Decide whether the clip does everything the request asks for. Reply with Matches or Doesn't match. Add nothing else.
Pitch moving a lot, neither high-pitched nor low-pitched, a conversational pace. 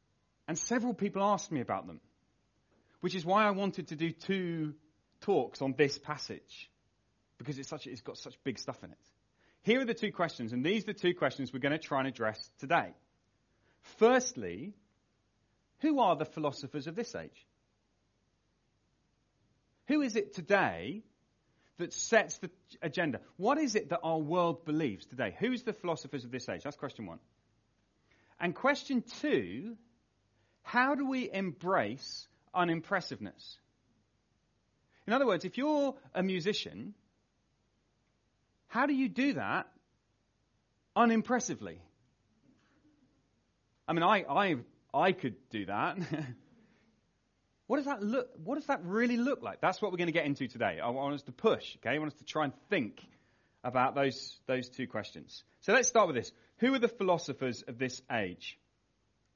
Matches